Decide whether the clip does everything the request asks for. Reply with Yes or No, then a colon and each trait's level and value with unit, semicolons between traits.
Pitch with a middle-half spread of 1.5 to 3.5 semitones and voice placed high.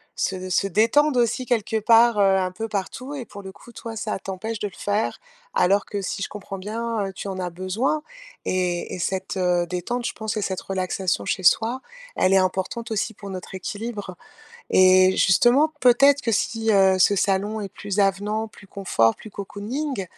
Yes: average, 3.2 semitones; high, 200 Hz